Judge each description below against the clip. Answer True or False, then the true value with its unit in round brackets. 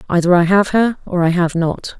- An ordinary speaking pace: False (240 wpm)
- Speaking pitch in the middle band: True (180 Hz)